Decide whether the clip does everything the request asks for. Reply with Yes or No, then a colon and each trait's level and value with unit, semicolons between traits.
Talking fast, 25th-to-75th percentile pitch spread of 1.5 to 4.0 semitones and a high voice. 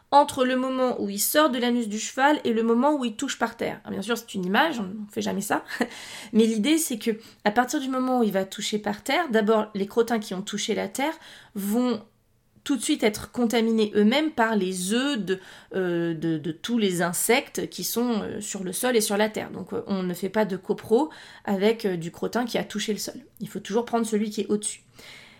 Yes: fast, 235 wpm; average, 3.3 semitones; high, 220 Hz